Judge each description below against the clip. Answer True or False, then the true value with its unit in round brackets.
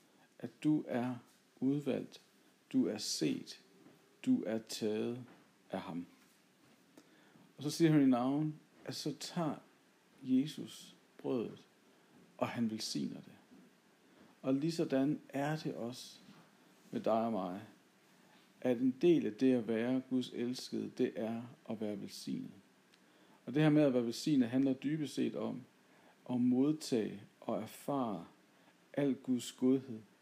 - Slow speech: True (135 wpm)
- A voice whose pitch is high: False (130 Hz)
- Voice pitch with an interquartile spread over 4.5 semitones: False (3.7 semitones)